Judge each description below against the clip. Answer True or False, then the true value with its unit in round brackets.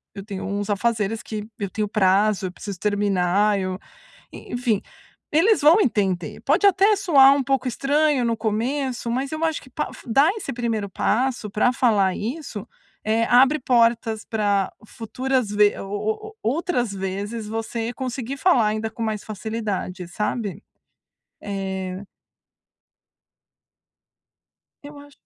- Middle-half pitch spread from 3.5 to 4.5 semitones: True (4.2 semitones)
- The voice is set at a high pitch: True (225 Hz)